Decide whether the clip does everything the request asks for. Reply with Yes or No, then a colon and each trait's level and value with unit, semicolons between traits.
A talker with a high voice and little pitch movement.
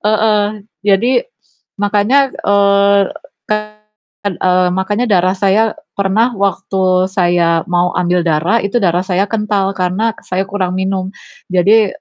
Yes: high, 195 Hz; narrow, 2.2 semitones